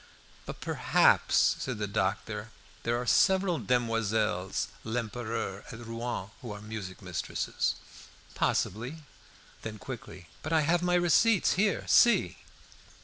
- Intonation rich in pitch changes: Yes, wide, 7.0 semitones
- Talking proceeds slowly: Yes, slow, 120 wpm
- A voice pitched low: Yes, low, 115 Hz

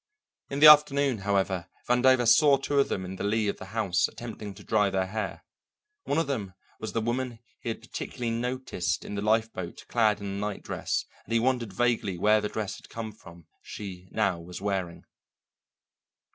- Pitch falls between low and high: No, low, 110 Hz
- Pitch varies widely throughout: No, average, 3.9 semitones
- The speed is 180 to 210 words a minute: Yes, average, 190 wpm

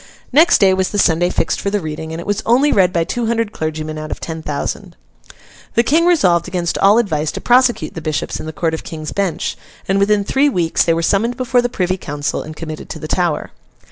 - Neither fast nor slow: No, fast, 235 wpm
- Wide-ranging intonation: Yes, wide, 6.0 semitones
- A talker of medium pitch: Yes, medium, 180 Hz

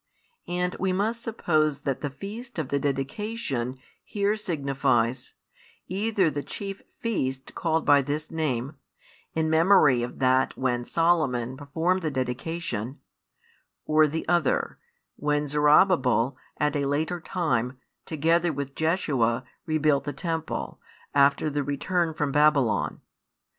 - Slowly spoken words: Yes, slow, 125 wpm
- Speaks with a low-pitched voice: No, medium, 150 Hz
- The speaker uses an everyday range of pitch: Yes, average, 4.1 semitones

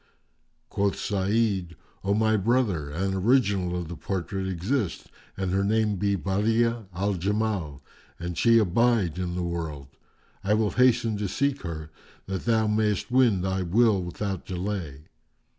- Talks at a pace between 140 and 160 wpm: Yes, average, 150 wpm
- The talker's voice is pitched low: Yes, low, 100 Hz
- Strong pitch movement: No, average, 3.7 semitones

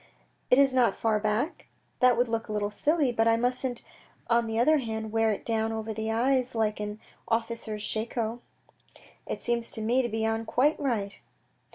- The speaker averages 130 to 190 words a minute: No, fast, 205 wpm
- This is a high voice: Yes, high, 225 Hz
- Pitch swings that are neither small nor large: No, narrow, 2.0 semitones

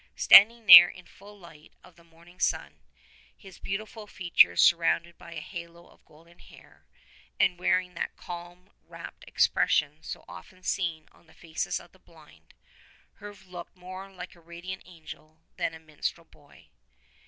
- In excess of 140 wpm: Yes, average, 160 wpm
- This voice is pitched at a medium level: Yes, medium, 175 Hz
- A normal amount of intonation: No, narrow, 2.2 semitones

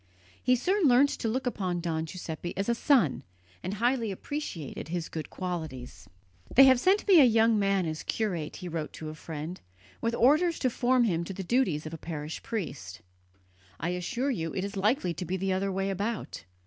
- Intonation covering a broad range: Yes, wide, 6.7 semitones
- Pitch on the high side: Yes, high, 195 Hz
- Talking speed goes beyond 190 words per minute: Yes, average, 200 wpm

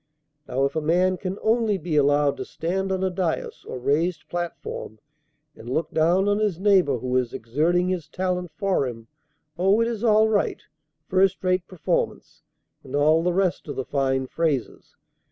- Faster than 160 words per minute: Yes, average, 175 wpm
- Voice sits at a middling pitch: Yes, medium, 175 Hz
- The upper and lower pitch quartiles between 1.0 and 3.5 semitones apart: No, average, 4.7 semitones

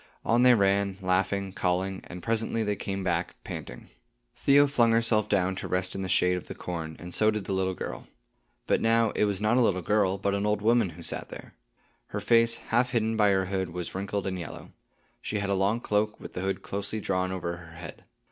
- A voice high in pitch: No, low, 100 Hz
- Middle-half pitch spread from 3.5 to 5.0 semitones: No, average, 2.7 semitones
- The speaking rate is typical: No, fast, 225 wpm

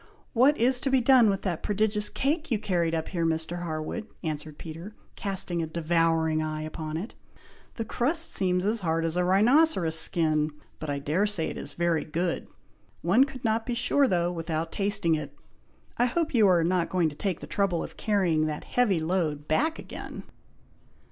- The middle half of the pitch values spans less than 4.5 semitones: No, average, 5.2 semitones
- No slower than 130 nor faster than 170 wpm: No, average, 190 wpm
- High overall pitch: No, medium, 175 Hz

